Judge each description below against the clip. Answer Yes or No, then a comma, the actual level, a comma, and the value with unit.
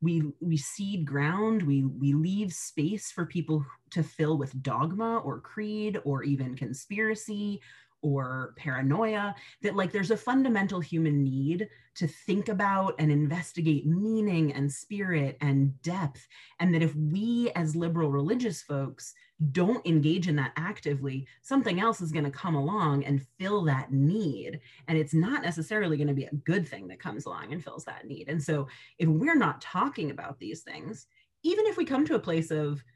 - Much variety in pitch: Yes, wide, 5.9 semitones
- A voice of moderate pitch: Yes, medium, 160 Hz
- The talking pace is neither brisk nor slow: Yes, average, 175 wpm